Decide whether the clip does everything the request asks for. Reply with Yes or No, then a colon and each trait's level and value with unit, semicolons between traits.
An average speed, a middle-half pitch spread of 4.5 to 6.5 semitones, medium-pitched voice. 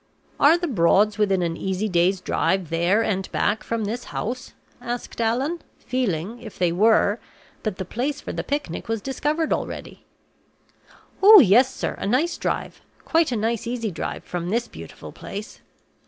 No: average, 165 wpm; average, 4.9 semitones; high, 220 Hz